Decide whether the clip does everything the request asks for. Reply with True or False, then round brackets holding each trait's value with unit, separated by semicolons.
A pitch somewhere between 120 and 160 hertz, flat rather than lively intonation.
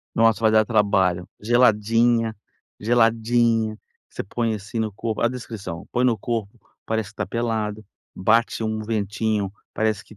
False (110 Hz; 1.6 semitones)